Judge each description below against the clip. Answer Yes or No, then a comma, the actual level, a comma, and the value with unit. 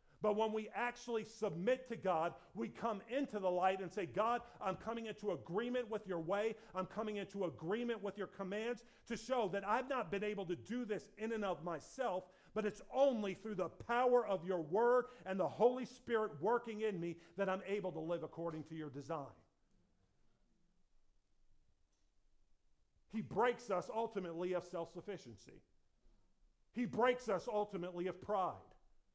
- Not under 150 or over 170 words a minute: Yes, average, 165 wpm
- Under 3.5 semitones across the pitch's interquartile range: No, average, 4.0 semitones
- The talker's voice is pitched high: Yes, high, 205 Hz